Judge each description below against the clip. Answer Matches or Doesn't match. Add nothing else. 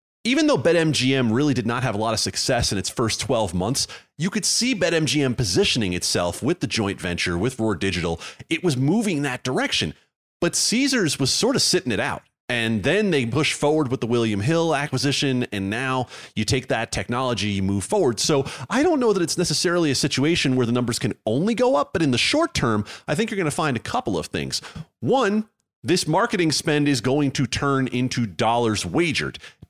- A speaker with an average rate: Doesn't match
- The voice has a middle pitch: Doesn't match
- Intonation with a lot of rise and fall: Matches